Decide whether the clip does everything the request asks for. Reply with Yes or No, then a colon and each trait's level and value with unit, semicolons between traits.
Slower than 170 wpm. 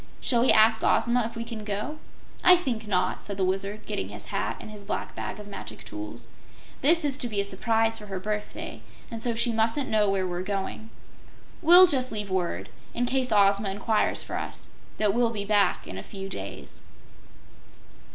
No: average, 195 wpm